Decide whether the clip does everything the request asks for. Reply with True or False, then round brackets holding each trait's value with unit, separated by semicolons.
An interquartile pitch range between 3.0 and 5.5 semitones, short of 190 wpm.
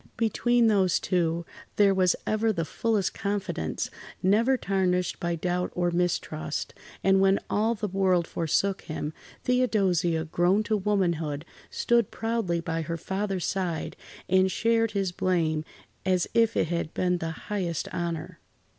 True (3.5 semitones; 140 wpm)